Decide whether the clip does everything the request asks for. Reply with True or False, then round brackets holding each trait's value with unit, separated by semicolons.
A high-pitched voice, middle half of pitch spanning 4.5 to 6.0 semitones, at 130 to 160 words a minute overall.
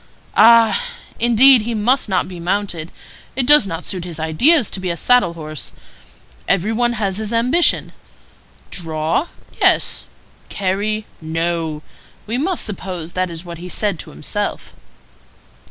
True (195 Hz; 5.6 semitones; 140 wpm)